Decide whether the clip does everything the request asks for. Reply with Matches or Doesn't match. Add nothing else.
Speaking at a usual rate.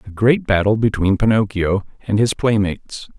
Matches